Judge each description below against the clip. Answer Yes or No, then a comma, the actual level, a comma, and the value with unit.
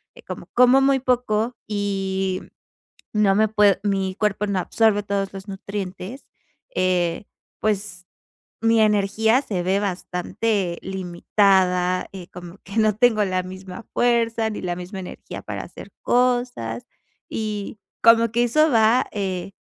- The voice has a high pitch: Yes, high, 205 Hz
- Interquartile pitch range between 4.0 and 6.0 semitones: No, average, 3.1 semitones